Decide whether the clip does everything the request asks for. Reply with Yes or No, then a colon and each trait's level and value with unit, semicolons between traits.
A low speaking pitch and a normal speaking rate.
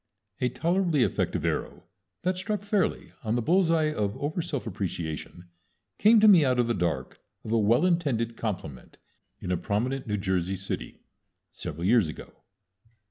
Yes: low, 120 Hz; average, 165 wpm